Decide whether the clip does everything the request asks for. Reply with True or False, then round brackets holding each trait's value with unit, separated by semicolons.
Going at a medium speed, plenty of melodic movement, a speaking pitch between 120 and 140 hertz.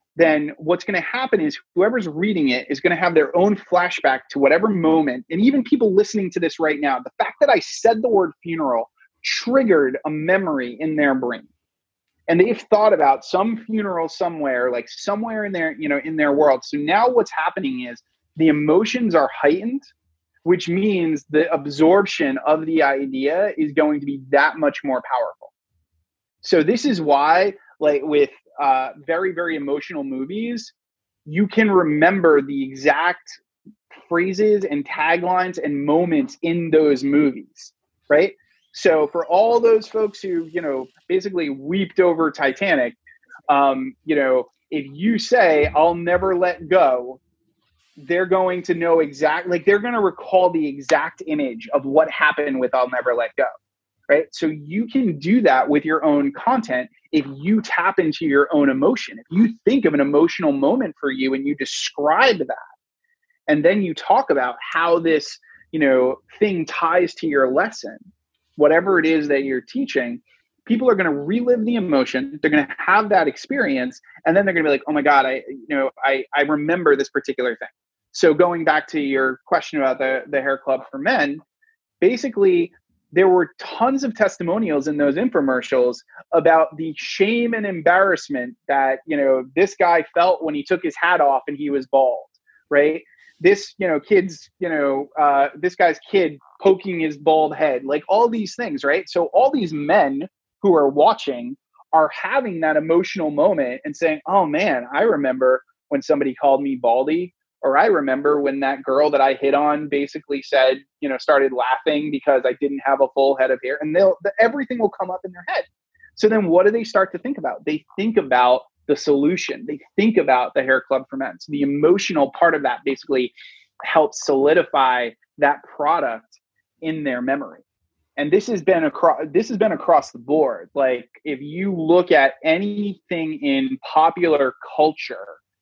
False (180 wpm; 6.3 semitones; 160 Hz)